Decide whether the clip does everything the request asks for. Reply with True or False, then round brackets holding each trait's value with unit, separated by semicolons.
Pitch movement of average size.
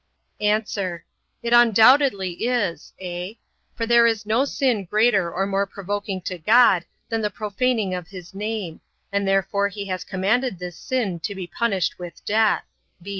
True (3.5 semitones)